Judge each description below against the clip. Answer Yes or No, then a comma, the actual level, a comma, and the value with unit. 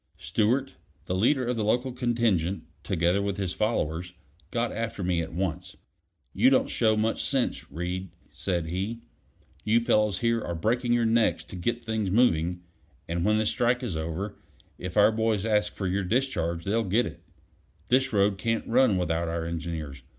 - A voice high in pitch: No, low, 105 Hz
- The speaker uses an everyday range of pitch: Yes, average, 4.7 semitones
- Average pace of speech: Yes, average, 170 wpm